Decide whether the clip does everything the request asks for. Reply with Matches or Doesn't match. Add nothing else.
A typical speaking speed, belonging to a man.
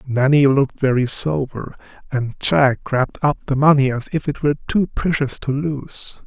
Matches